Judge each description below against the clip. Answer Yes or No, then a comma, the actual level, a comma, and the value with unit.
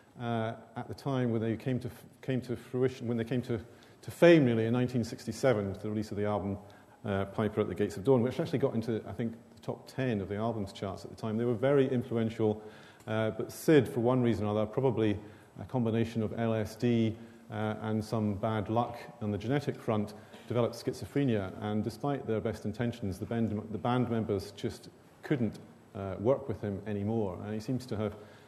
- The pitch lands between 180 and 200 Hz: No, low, 115 Hz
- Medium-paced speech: No, fast, 210 wpm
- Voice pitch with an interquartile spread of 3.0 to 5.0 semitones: No, narrow, 2.5 semitones